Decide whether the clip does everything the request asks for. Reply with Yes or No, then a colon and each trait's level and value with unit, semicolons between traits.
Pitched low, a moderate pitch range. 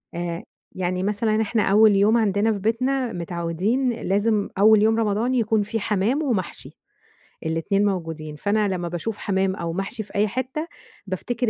No: high, 205 Hz; average, 3.1 semitones